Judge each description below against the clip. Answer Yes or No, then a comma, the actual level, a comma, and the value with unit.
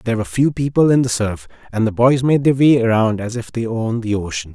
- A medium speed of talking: No, fast, 265 wpm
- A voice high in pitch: No, low, 115 Hz